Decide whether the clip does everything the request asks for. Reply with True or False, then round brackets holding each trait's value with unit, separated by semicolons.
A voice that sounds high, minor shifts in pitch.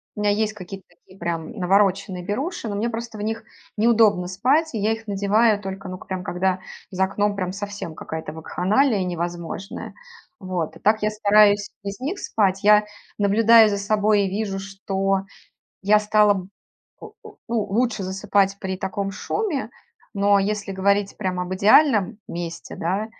True (200 Hz; 2.1 semitones)